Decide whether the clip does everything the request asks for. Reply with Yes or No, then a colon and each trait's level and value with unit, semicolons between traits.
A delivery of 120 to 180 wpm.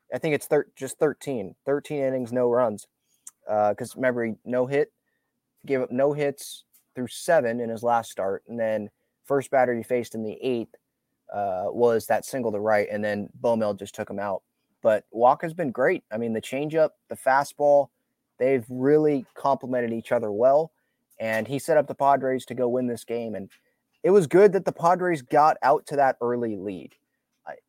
No: average, 190 wpm